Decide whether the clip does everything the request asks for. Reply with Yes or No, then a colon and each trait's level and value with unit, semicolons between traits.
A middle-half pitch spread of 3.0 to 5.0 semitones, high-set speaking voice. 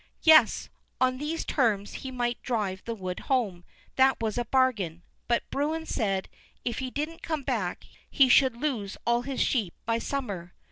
Yes: average, 4.7 semitones; high, 245 Hz